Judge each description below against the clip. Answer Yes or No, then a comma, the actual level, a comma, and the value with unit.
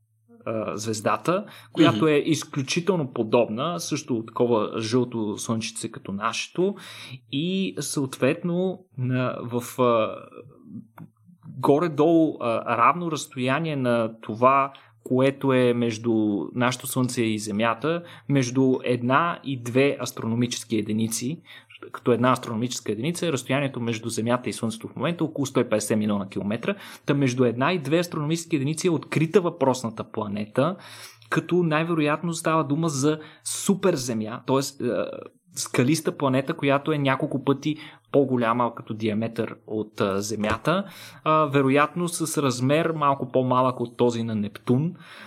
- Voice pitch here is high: No, low, 130 Hz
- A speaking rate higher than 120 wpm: No, slow, 115 wpm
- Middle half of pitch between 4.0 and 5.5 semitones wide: Yes, average, 4.9 semitones